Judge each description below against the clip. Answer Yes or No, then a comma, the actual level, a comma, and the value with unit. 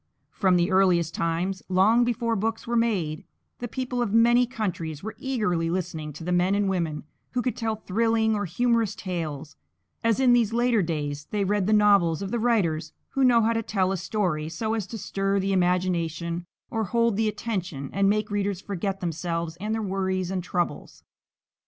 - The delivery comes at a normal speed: Yes, average, 190 wpm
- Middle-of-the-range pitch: No, high, 195 Hz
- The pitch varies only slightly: No, average, 4.5 semitones